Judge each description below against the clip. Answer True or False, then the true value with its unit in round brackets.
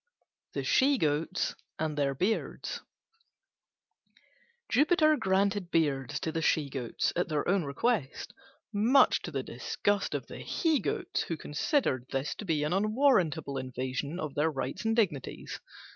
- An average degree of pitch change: False (6.9 semitones)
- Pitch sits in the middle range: True (160 Hz)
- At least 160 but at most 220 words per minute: False (145 wpm)